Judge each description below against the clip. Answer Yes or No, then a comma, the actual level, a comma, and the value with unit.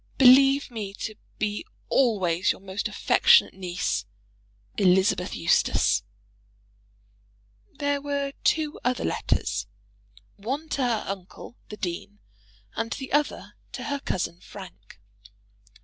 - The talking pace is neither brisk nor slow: No, slow, 115 wpm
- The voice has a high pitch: Yes, high, 215 Hz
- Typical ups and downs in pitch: No, wide, 6.5 semitones